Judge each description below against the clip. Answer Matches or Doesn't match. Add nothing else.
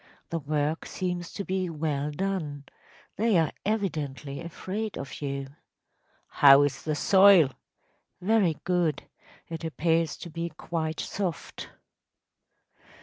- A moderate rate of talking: Doesn't match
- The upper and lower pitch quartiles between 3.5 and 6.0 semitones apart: Matches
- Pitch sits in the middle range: Matches